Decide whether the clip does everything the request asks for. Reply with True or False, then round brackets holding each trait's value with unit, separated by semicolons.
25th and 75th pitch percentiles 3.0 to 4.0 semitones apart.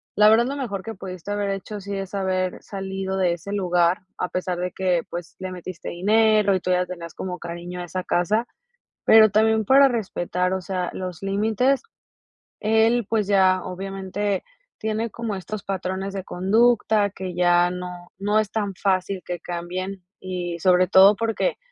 False (2.6 semitones)